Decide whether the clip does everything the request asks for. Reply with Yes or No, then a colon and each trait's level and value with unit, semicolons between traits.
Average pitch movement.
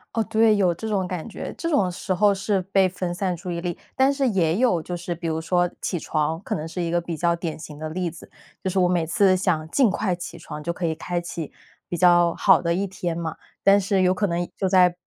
No: narrow, 2.2 semitones